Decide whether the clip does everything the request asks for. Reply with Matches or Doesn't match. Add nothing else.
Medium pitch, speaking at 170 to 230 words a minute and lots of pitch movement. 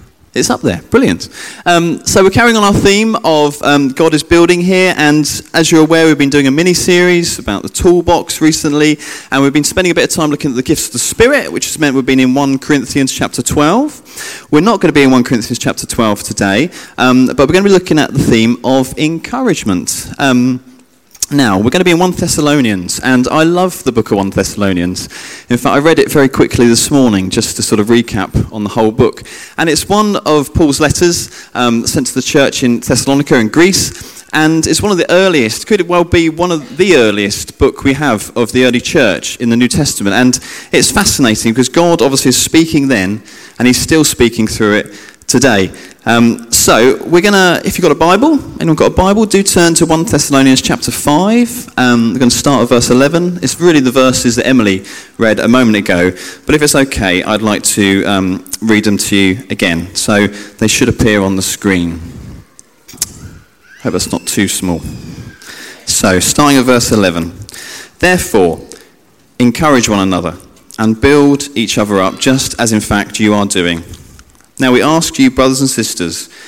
Doesn't match